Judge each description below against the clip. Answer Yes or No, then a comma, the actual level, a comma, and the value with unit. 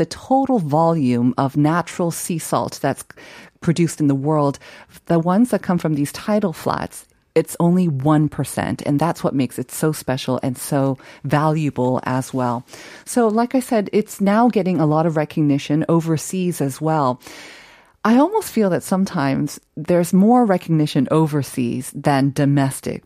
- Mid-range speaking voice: Yes, medium, 155 Hz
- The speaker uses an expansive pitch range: No, average, 4.6 semitones